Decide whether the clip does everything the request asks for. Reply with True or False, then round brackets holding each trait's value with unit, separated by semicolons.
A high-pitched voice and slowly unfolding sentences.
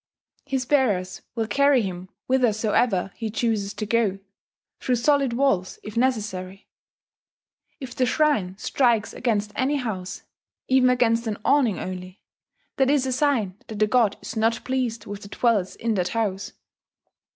False (225 Hz; 150 wpm)